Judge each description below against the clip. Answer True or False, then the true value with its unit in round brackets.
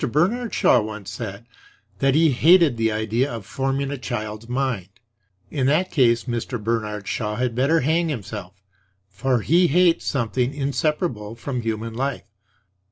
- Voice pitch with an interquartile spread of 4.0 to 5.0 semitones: True (4.5 semitones)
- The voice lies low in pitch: True (125 Hz)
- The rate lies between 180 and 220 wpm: False (150 wpm)